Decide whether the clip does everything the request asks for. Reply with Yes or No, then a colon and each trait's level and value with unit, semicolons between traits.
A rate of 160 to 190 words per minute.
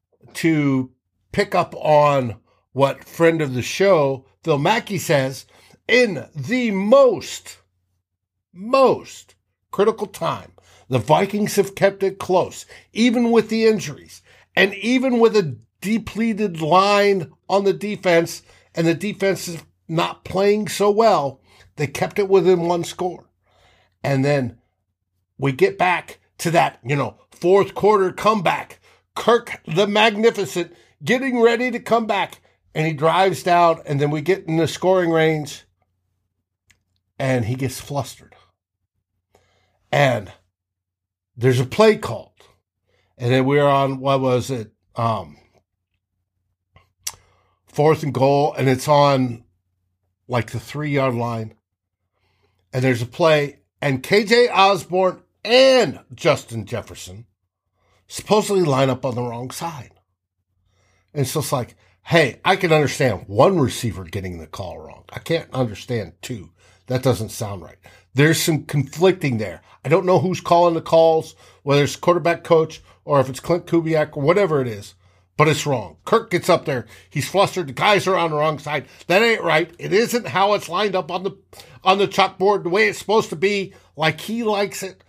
No: average, 150 wpm